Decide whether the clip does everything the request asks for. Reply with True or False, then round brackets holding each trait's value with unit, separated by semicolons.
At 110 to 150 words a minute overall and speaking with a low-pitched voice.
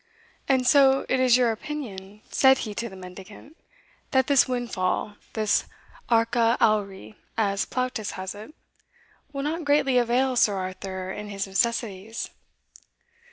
False (135 wpm; 230 Hz)